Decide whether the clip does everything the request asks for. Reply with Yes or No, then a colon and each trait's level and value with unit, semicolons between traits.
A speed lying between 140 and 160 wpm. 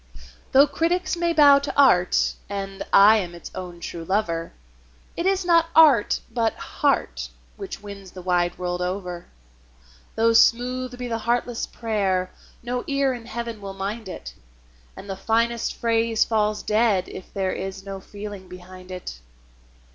Yes: average, 155 wpm